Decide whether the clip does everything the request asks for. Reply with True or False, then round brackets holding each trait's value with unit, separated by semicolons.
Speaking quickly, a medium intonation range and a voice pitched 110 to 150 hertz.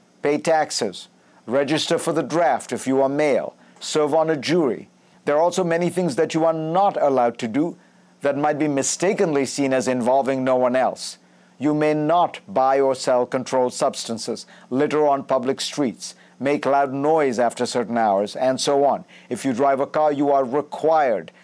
False (180 wpm; 3.1 semitones; 140 Hz)